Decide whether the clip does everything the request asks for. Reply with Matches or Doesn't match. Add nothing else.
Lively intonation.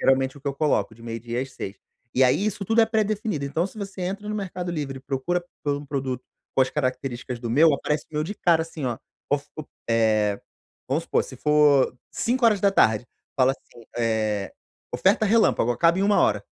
Matches